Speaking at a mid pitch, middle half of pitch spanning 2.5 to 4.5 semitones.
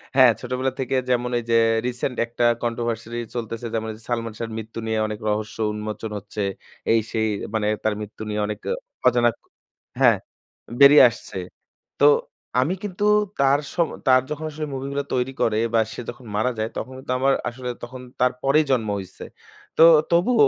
No: low, 120 Hz; average, 3.1 semitones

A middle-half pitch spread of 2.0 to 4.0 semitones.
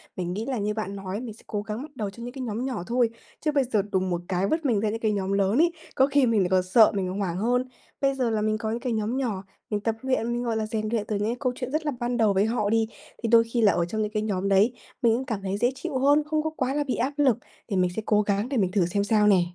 Yes: average, 3.7 semitones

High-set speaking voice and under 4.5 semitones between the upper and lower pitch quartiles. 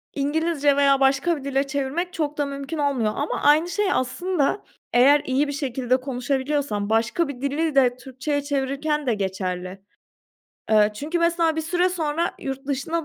Yes: very high, 280 Hz; average, 3.0 semitones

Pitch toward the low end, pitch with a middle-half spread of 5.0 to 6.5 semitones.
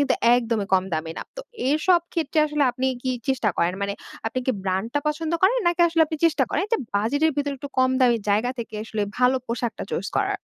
No: very high, 255 Hz; average, 5.3 semitones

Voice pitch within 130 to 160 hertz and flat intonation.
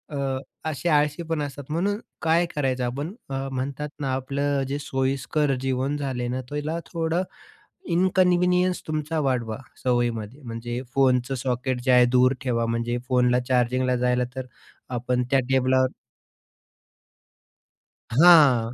No: low, 135 Hz; average, 3.0 semitones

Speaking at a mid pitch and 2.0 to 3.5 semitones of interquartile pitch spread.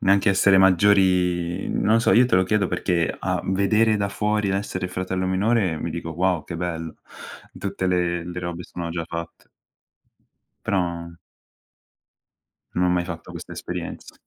No: very low, 90 Hz; narrow, 2.3 semitones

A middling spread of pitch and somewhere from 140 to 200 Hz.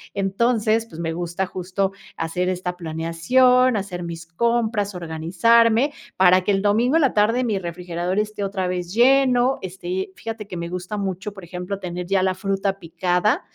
Yes: average, 3.7 semitones; high, 190 Hz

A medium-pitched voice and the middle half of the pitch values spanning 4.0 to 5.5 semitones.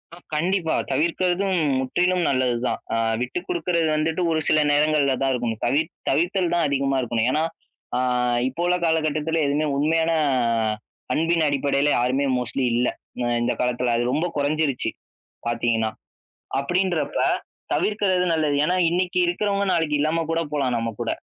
Yes: medium, 155 Hz; average, 4.6 semitones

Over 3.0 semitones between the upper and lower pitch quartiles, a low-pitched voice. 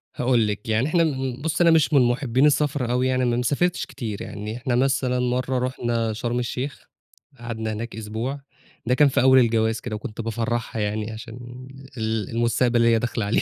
No: narrow, 2.6 semitones; low, 120 Hz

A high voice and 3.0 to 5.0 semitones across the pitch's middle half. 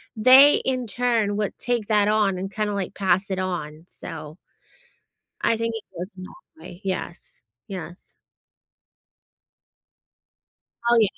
Yes: high, 205 Hz; average, 3.6 semitones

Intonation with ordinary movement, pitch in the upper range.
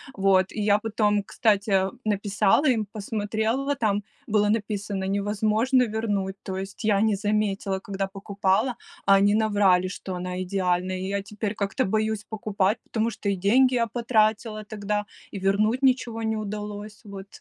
No: narrow, 1.9 semitones; high, 210 Hz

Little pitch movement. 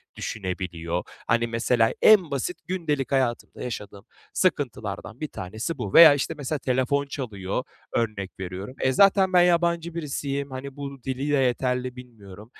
No: average, 4.9 semitones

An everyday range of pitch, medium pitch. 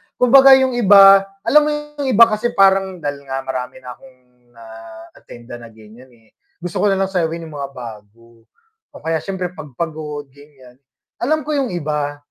No: wide, 7.8 semitones; medium, 150 Hz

